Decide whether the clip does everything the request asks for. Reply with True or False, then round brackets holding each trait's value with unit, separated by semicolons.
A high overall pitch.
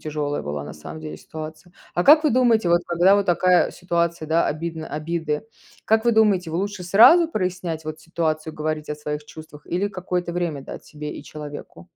False (170 Hz)